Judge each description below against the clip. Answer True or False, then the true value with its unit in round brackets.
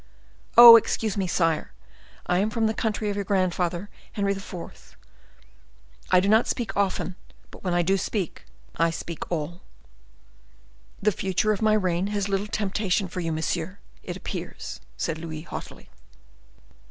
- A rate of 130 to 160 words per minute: True (155 wpm)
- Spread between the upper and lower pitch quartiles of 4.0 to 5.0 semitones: False (3.2 semitones)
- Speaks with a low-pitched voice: False (190 Hz)